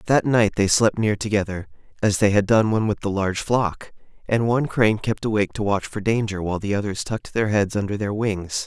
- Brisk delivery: Yes, fast, 230 wpm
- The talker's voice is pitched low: Yes, low, 105 Hz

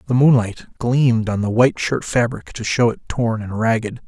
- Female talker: No, male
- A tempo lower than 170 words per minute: No, fast, 205 wpm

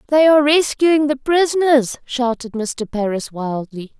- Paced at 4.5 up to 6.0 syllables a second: No, 4.3 syllables/s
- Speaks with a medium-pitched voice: No, very high, 265 Hz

